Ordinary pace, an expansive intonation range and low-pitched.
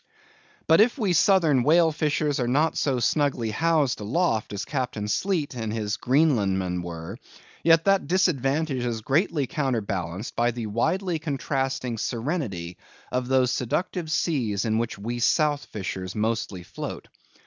Yes: average, 145 wpm; wide, 6.4 semitones; low, 130 Hz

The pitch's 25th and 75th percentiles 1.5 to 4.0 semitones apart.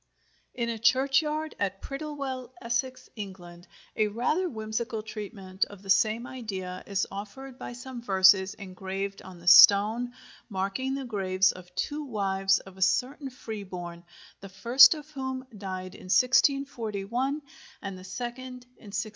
No: average, 5.1 semitones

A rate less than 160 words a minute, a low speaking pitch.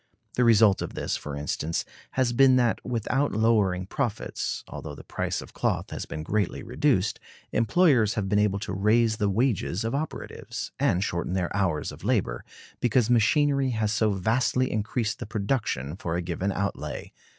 No: average, 170 wpm; low, 110 Hz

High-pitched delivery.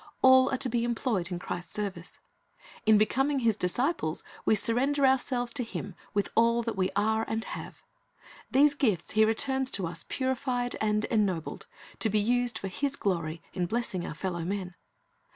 Yes: high, 220 Hz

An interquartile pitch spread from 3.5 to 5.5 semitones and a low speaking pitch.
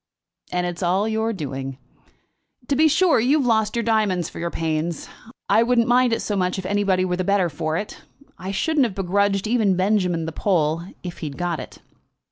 No: average, 4.2 semitones; high, 195 Hz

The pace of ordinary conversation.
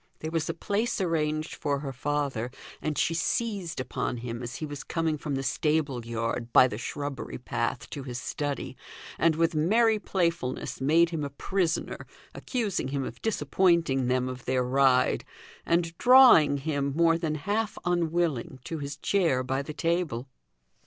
Yes: average, 165 wpm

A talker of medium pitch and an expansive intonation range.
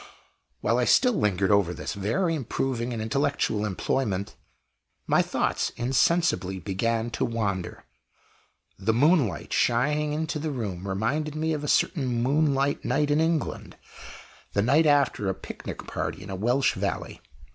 No: low, 125 Hz; wide, 6.5 semitones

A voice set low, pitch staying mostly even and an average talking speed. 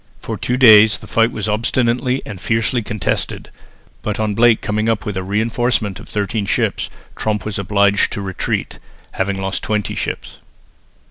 Yes: low, 105 Hz; narrow, 2.2 semitones; average, 165 wpm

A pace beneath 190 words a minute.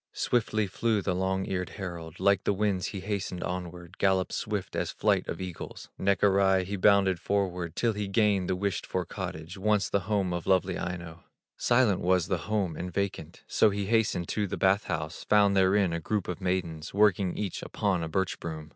No: average, 195 wpm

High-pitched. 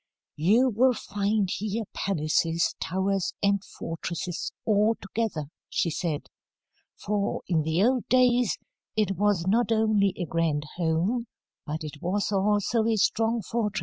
Yes: high, 200 Hz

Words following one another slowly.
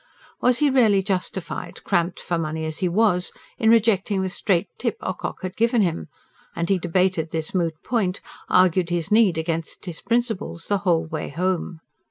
No: average, 175 wpm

